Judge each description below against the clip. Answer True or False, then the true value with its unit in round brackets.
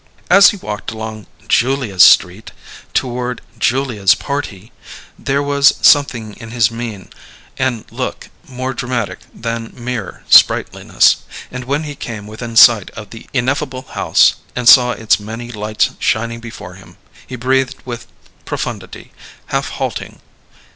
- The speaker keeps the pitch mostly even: False (3.0 semitones)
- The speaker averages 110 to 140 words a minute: True (135 wpm)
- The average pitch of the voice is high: False (120 Hz)